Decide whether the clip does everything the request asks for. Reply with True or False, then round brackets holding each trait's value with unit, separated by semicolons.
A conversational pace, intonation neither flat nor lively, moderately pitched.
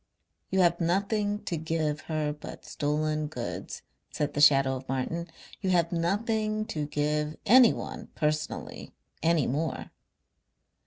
False (125 wpm; 3.7 semitones; 155 Hz)